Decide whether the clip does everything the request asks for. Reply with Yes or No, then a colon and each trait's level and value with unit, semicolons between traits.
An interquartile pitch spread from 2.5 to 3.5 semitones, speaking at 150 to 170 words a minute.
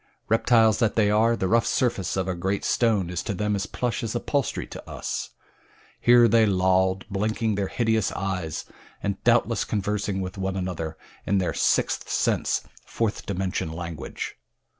Yes: average, 3.2 semitones; average, 160 wpm